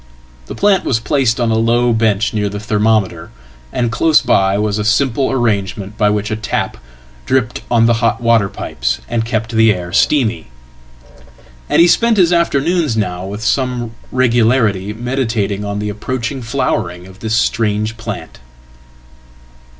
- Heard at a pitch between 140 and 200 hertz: No, low, 115 Hz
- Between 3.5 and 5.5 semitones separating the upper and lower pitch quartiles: No, average, 3.1 semitones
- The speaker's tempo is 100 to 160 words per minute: Yes, average, 140 wpm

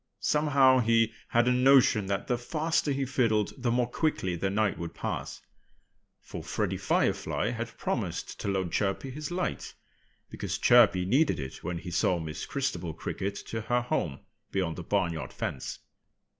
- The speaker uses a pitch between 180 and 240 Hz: No, low, 115 Hz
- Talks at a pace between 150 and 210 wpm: Yes, average, 160 wpm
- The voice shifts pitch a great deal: Yes, wide, 5.7 semitones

